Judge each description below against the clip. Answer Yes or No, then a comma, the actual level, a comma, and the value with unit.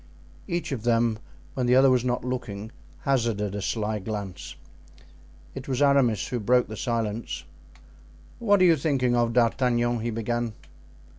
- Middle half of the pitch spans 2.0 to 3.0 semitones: Yes, average, 2.7 semitones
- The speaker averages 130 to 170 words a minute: Yes, average, 150 wpm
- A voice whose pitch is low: Yes, low, 120 Hz